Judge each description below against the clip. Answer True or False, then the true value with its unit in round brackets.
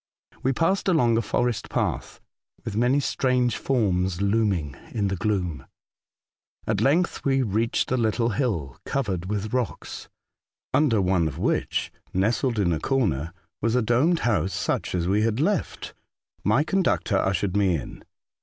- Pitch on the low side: True (110 Hz)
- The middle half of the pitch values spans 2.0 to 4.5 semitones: False (5.0 semitones)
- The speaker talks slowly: False (155 wpm)